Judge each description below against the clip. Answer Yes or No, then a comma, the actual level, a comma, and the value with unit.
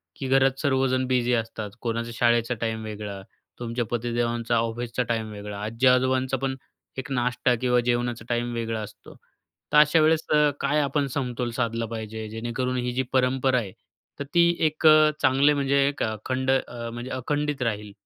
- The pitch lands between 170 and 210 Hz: No, low, 125 Hz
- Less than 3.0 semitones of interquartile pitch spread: Yes, narrow, 2.4 semitones